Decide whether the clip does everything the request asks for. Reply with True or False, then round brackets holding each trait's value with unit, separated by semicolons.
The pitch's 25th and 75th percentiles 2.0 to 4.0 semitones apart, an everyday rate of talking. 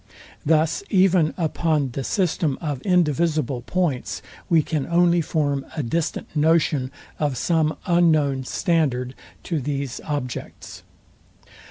False (3.3 semitones; 115 wpm)